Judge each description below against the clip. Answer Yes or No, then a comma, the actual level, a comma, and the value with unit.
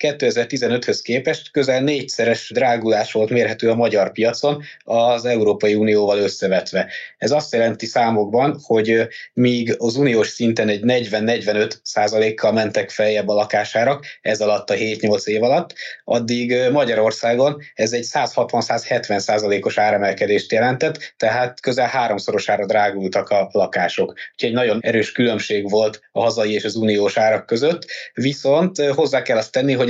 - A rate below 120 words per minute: No, average, 140 wpm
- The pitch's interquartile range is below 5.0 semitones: Yes, narrow, 2.6 semitones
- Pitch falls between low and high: No, low, 115 Hz